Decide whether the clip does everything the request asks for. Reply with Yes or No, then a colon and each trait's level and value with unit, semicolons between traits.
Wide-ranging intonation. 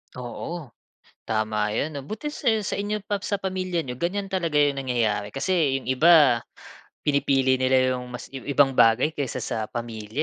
Yes: wide, 6.0 semitones